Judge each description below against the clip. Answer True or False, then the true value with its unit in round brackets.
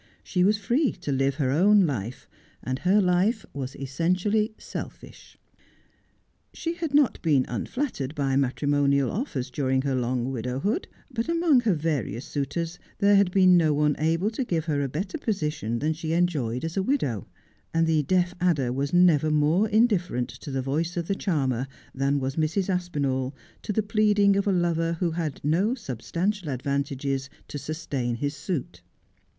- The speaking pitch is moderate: True (160 Hz)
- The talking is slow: False (165 wpm)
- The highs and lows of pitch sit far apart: True (6.0 semitones)